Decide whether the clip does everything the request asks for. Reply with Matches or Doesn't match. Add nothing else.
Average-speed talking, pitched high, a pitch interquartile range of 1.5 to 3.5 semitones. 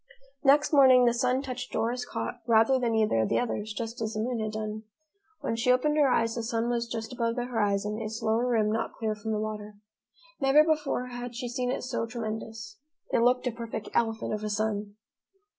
Doesn't match